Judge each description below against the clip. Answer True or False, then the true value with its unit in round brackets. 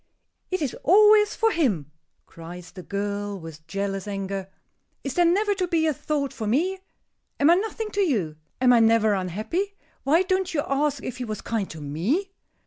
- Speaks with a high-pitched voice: True (255 Hz)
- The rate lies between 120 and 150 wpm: False (185 wpm)